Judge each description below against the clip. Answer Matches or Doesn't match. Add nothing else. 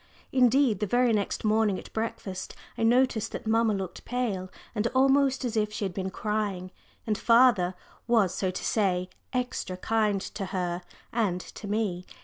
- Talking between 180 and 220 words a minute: Doesn't match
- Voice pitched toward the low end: Doesn't match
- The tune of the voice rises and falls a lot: Doesn't match